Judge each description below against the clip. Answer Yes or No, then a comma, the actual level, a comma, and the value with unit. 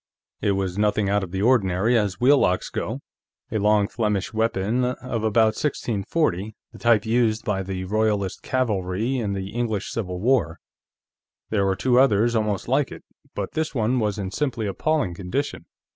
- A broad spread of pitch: No, average, 3.5 semitones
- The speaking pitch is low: Yes, low, 105 Hz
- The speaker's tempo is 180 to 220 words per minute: No, average, 170 wpm